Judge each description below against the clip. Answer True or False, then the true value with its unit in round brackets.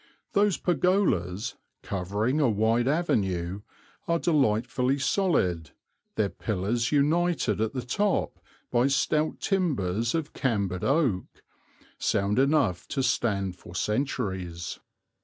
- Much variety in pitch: True (7.5 semitones)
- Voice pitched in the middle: False (120 Hz)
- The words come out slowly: True (105 wpm)